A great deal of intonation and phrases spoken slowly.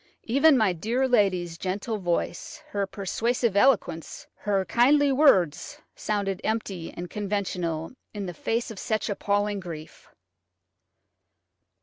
No: average, 4.1 semitones; slow, 115 wpm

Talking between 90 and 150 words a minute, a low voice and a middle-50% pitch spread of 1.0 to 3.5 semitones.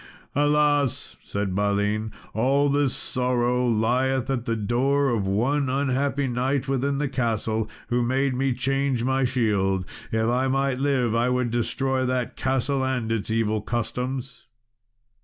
Yes: average, 140 wpm; low, 125 Hz; average, 2.9 semitones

